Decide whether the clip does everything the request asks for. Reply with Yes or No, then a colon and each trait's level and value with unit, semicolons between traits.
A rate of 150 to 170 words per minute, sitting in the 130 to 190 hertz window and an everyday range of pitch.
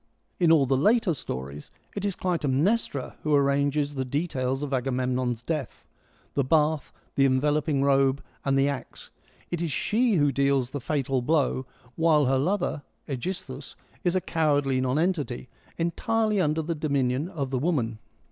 Yes: average, 155 wpm; medium, 140 Hz; average, 3.7 semitones